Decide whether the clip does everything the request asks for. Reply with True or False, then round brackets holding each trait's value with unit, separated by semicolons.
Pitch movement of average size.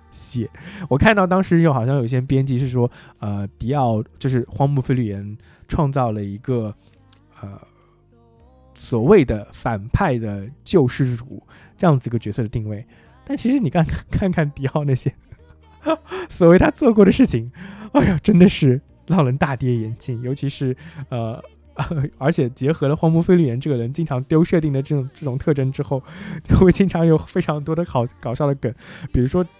False (5.9 semitones)